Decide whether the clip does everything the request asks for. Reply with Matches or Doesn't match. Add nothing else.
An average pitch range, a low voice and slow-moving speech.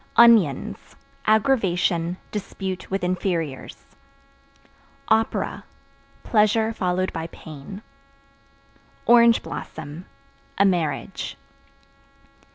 Doesn't match